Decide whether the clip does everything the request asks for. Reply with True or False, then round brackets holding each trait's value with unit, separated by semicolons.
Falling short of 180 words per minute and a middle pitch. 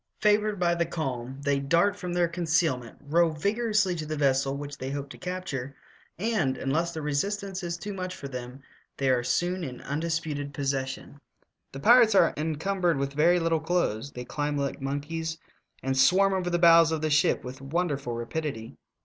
False (185 wpm; 155 Hz)